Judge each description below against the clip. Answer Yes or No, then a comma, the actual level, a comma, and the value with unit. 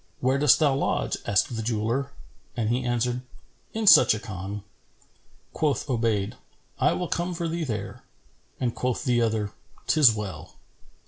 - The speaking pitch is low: Yes, low, 120 Hz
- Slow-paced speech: No, average, 150 wpm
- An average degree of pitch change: Yes, average, 4.4 semitones